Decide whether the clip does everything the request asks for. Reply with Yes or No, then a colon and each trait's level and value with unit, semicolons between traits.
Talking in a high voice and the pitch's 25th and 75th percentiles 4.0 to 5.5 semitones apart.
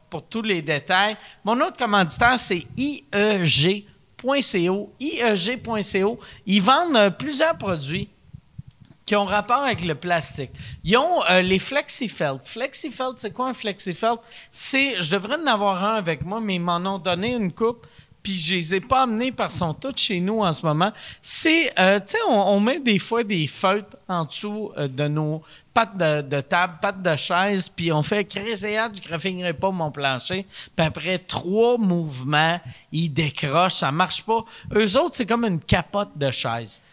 Yes: high, 195 Hz; average, 5.1 semitones